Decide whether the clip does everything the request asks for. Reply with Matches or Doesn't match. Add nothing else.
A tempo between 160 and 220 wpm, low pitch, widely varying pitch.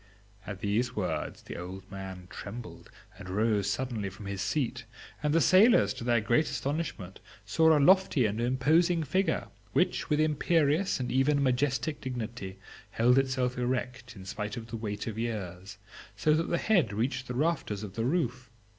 Matches